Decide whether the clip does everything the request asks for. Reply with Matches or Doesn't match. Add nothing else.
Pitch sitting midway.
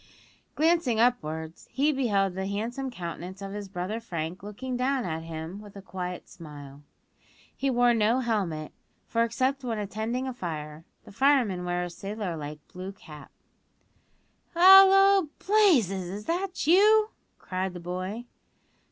Doesn't match